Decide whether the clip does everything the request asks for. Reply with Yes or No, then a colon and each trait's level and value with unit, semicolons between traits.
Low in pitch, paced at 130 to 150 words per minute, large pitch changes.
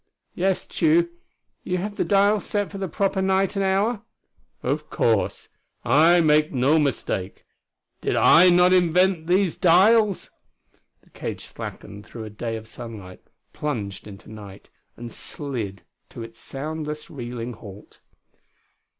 No: medium, 155 Hz; average, 140 wpm; wide, 8.6 semitones